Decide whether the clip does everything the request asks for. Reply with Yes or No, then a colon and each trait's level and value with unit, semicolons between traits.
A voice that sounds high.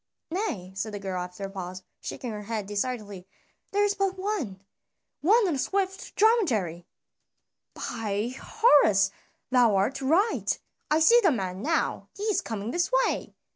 Yes: high, 245 Hz